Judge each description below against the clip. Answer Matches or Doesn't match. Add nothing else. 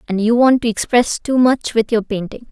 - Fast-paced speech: Matches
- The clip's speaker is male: Doesn't match